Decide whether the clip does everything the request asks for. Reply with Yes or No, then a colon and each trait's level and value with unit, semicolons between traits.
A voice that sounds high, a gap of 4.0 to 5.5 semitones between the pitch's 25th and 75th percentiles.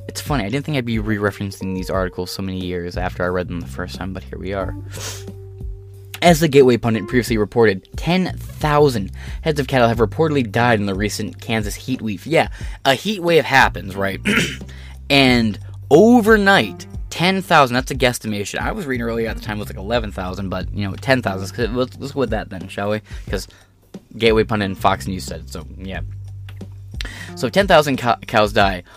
No: low, 105 Hz; average, 4.4 semitones